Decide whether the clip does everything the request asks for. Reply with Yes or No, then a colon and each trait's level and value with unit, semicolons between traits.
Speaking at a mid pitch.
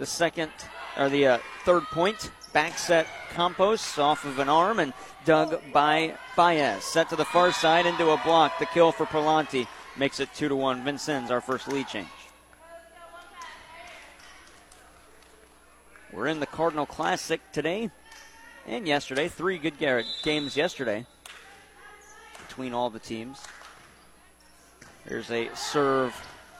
Yes: medium, 160 Hz